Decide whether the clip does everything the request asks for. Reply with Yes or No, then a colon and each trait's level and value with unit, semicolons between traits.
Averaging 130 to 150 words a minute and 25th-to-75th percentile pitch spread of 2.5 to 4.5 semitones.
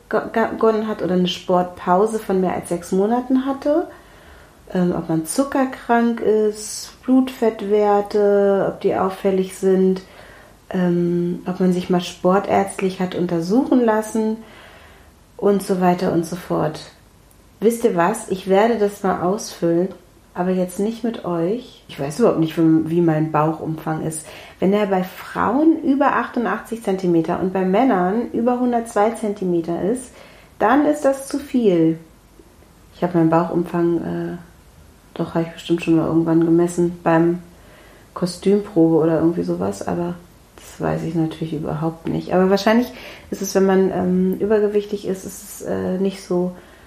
Yes: average, 145 wpm; average, 4.0 semitones